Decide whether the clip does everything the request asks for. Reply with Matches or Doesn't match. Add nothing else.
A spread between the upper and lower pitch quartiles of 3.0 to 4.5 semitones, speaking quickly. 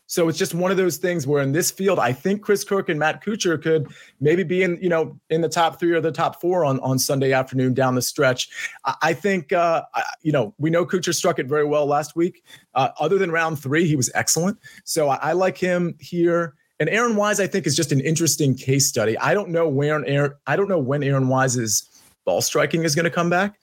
Matches